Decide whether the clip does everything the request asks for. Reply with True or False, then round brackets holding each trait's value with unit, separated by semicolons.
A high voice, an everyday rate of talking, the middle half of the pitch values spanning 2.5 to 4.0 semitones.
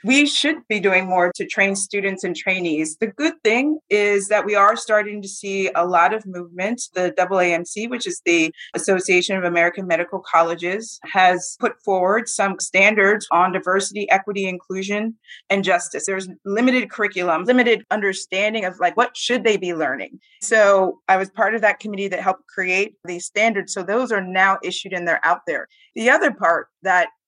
True (195 Hz; 180 wpm; 2.9 semitones)